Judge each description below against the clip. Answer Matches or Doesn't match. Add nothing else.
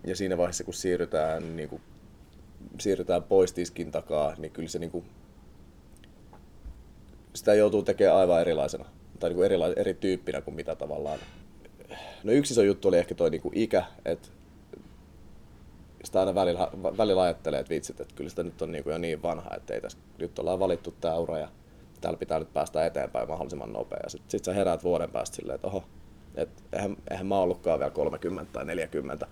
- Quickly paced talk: Matches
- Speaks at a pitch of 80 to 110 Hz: Matches